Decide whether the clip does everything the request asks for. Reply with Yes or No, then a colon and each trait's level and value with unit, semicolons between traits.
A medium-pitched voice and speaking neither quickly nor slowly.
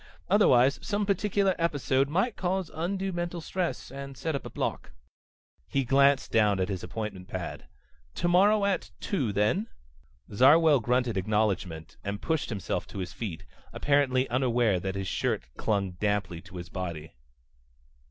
No: low, 130 Hz; average, 145 wpm